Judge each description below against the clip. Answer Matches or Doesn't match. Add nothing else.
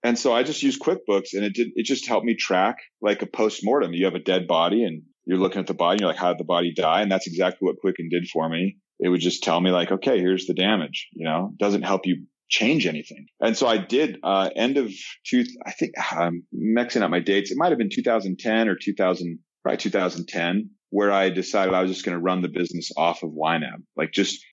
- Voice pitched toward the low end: Matches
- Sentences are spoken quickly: Matches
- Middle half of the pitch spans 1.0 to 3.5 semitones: Matches